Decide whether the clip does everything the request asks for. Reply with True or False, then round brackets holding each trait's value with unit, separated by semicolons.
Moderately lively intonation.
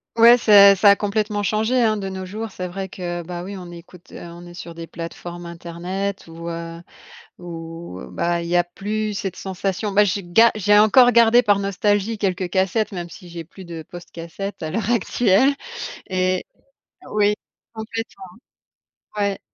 True (3.2 semitones)